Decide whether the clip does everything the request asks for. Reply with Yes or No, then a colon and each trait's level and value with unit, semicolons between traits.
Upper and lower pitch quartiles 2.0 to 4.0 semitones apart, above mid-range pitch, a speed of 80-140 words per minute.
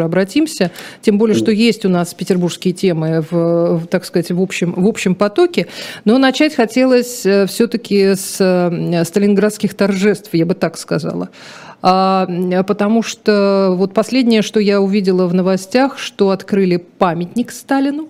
Yes: average, 3.4 semitones; high, 195 Hz; average, 135 wpm